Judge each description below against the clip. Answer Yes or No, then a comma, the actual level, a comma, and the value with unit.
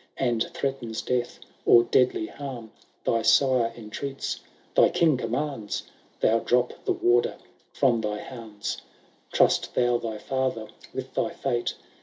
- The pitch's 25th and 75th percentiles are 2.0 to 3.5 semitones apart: Yes, average, 2.7 semitones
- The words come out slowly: Yes, slow, 130 wpm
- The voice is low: Yes, low, 120 Hz